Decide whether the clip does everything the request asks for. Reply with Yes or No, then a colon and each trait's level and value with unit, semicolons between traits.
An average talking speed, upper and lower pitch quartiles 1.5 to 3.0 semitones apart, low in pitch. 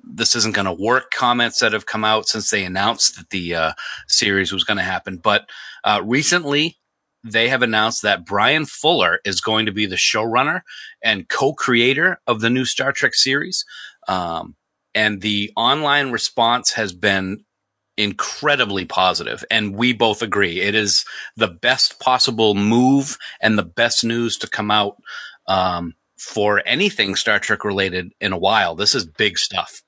Yes: average, 170 wpm; average, 2.7 semitones; low, 110 Hz